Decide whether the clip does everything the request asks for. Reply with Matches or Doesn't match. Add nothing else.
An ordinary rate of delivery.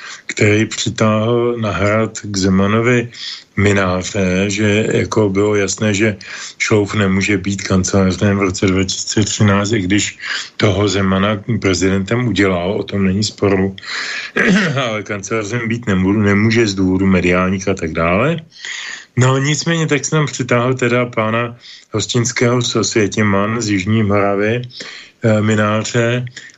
Matches